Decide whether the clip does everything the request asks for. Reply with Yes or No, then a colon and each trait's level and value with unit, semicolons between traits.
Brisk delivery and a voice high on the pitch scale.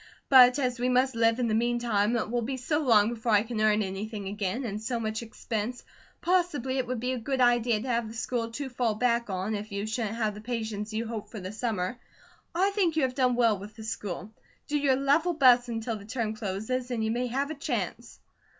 Yes: fast, 235 wpm; high, 235 Hz